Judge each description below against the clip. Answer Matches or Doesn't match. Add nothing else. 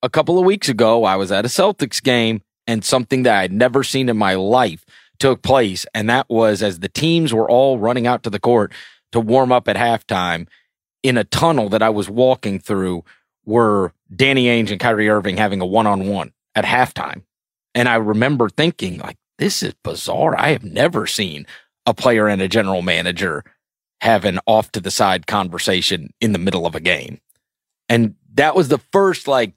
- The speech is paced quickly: Doesn't match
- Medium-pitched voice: Doesn't match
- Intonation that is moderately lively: Matches